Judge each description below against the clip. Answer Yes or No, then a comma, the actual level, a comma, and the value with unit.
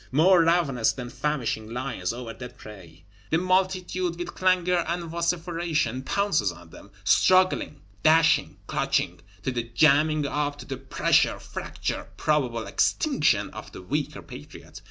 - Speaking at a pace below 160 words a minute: Yes, average, 140 wpm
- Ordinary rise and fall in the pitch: No, wide, 6.0 semitones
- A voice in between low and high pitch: Yes, medium, 150 Hz